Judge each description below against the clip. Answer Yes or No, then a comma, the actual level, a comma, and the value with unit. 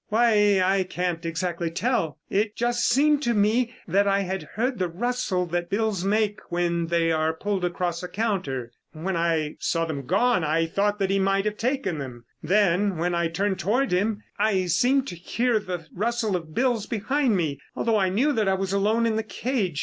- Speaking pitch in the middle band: No, high, 195 Hz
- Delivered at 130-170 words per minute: No, average, 195 wpm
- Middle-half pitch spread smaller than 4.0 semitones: No, average, 4.5 semitones